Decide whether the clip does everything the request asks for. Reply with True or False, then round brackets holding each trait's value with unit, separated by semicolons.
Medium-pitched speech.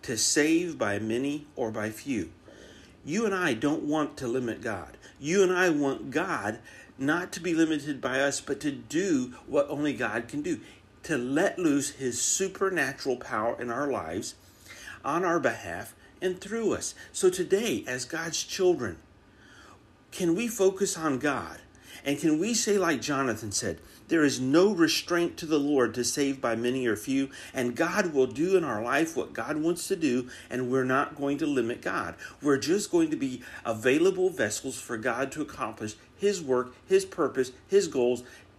True (145 Hz)